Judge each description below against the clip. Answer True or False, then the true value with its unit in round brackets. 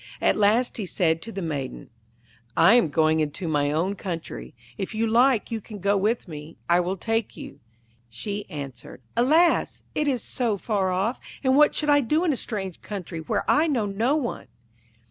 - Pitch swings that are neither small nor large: False (6.3 semitones)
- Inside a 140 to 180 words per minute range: False (190 wpm)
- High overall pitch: True (205 Hz)